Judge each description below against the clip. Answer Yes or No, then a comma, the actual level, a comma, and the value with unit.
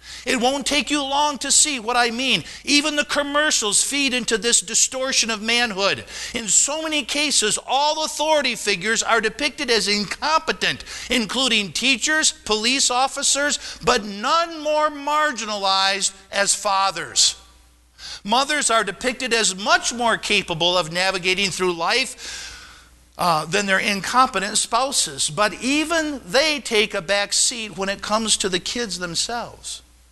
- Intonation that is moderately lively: No, wide, 6.2 semitones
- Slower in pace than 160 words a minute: Yes, average, 140 wpm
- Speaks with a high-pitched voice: Yes, high, 235 Hz